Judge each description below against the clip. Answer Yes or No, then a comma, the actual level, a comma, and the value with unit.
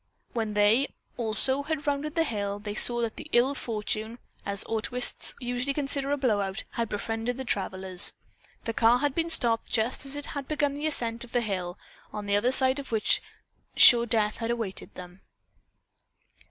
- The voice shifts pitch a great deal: No, average, 4.4 semitones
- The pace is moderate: Yes, average, 180 wpm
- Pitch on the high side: Yes, high, 235 Hz